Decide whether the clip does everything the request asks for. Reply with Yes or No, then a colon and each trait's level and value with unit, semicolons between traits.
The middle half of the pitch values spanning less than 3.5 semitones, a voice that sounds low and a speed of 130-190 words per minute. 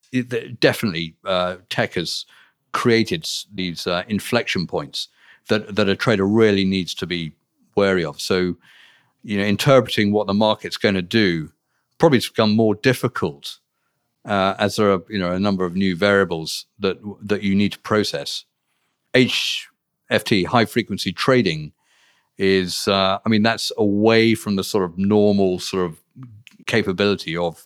Yes: narrow, 2.6 semitones; low, 100 Hz; average, 155 wpm